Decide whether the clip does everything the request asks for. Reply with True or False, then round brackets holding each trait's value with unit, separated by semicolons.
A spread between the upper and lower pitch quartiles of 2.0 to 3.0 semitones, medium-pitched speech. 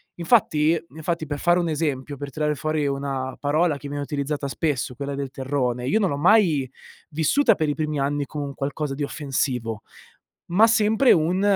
True (2.7 semitones; 145 Hz)